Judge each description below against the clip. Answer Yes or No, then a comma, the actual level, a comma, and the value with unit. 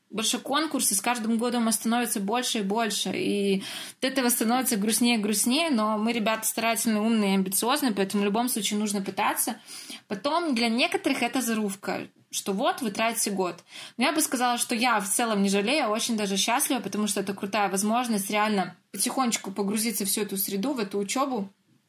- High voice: Yes, high, 225 Hz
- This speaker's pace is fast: Yes, fast, 185 wpm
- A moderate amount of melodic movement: Yes, average, 3.2 semitones